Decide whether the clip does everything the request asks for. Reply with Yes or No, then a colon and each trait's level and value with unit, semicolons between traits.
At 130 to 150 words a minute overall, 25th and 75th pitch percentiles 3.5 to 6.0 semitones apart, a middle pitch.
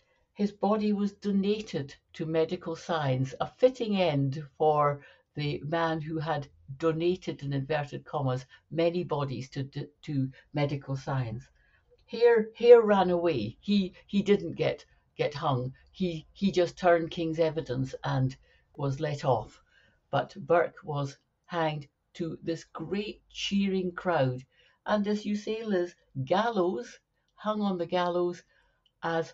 Yes: slow, 135 wpm; average, 4.7 semitones; medium, 165 Hz